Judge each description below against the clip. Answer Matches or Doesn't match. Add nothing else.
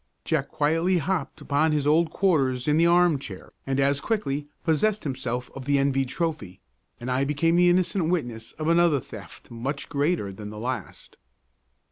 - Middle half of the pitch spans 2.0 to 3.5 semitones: Doesn't match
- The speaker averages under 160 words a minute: Doesn't match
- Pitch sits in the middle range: Matches